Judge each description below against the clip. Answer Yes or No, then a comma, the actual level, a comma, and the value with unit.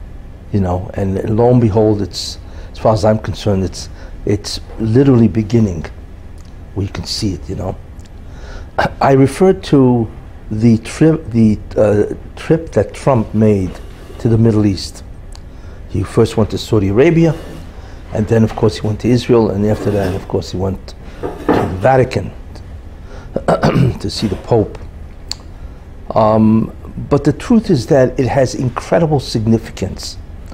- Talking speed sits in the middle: Yes, average, 150 wpm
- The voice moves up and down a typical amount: Yes, average, 4.6 semitones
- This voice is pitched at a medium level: No, low, 100 Hz